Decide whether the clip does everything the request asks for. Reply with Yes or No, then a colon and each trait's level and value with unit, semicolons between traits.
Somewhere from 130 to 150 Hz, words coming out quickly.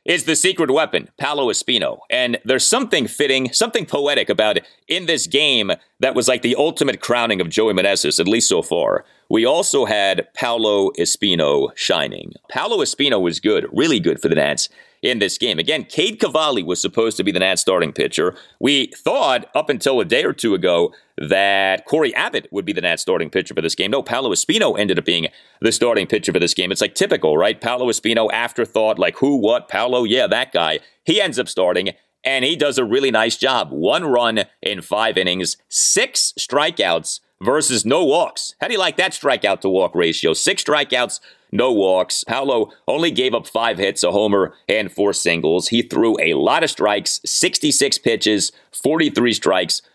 No: low, 135 Hz; average, 195 wpm